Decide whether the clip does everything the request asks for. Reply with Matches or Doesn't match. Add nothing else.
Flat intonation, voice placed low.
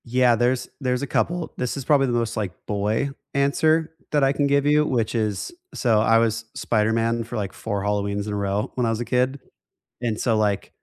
Doesn't match